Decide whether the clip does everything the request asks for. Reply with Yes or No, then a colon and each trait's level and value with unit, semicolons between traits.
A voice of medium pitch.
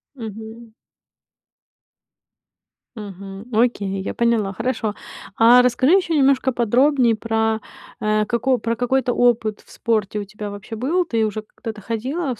No: high, 230 Hz